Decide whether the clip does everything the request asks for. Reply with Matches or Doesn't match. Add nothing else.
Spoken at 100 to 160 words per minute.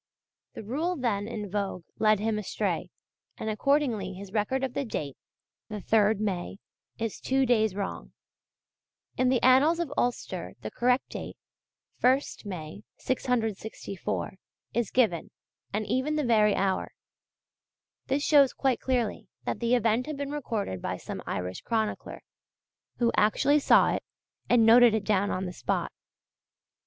Matches